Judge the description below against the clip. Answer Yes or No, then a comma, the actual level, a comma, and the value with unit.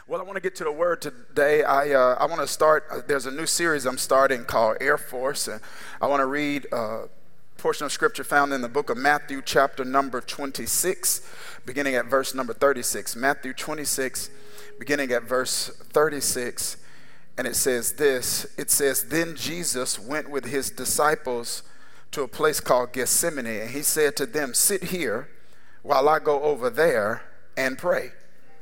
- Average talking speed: Yes, average, 180 wpm